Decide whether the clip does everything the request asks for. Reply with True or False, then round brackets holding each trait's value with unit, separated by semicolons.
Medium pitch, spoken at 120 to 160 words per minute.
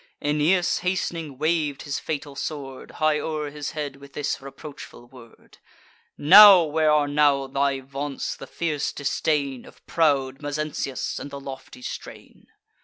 True (145 Hz; 140 wpm)